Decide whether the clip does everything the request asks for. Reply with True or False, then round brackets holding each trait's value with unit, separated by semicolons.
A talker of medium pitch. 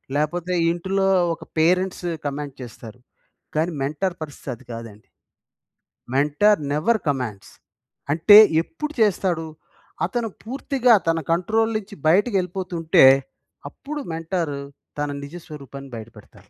True (165 Hz)